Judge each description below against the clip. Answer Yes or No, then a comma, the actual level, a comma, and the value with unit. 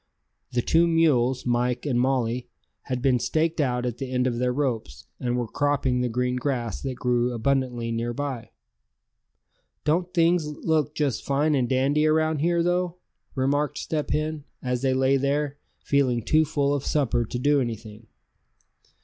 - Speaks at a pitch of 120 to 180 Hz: Yes, low, 135 Hz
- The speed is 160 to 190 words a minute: Yes, average, 165 wpm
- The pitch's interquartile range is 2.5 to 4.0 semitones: Yes, average, 3.4 semitones